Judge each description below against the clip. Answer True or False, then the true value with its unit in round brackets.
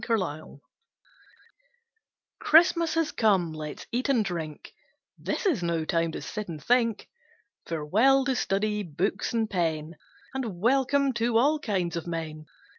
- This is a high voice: True (205 Hz)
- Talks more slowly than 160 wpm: True (135 wpm)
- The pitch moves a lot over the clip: True (7.3 semitones)